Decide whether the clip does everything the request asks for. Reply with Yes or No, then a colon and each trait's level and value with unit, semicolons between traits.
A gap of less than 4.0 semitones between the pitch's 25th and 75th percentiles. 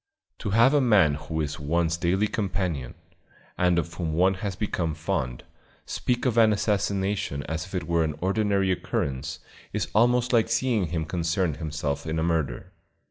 No: average, 4.6 semitones